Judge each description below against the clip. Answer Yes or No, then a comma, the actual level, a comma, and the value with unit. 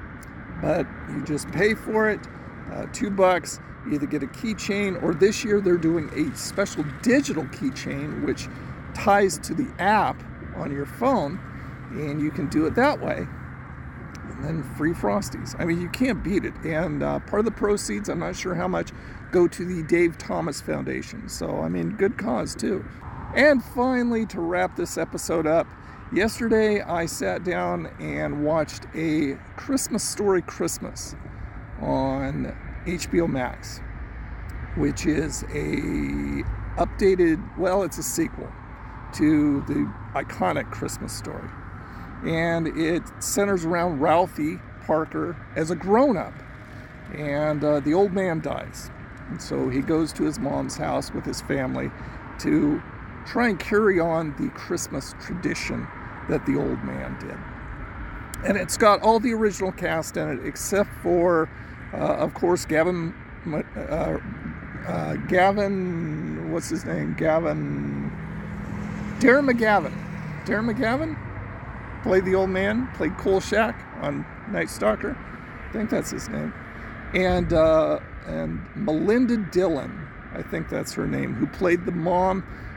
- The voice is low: No, medium, 170 Hz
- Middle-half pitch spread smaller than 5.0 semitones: No, wide, 5.4 semitones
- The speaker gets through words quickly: No, average, 145 wpm